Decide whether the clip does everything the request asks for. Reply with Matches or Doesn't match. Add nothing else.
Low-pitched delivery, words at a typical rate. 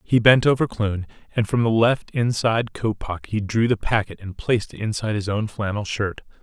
Doesn't match